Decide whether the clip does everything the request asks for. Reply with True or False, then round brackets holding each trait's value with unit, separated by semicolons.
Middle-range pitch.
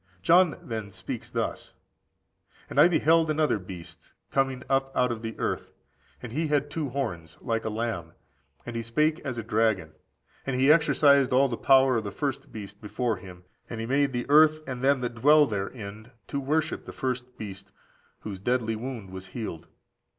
False (125 Hz)